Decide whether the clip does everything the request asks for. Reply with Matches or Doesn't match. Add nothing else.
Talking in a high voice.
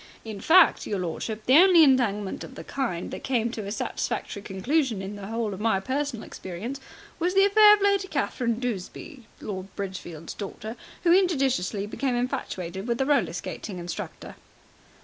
Matches